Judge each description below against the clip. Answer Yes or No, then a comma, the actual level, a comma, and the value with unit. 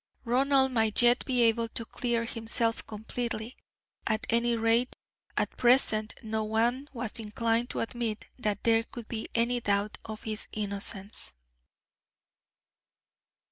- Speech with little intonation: Yes, narrow, 1.7 semitones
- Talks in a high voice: Yes, high, 230 Hz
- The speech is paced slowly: Yes, slow, 130 wpm